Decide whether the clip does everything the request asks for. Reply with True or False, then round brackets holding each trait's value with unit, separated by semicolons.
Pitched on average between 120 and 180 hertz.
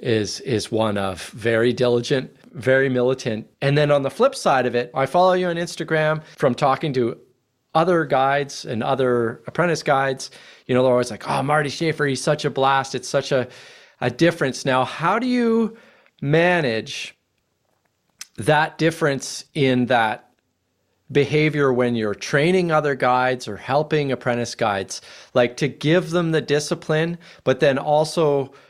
True (135 Hz)